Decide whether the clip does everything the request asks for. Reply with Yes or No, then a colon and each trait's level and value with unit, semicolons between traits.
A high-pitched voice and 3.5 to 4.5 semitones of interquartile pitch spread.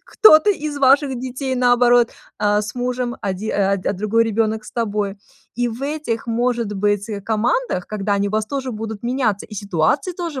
Yes: high, 230 Hz; average, 3.8 semitones